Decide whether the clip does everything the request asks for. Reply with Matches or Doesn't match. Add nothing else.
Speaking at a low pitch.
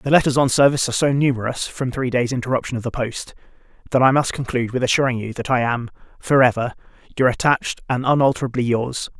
Matches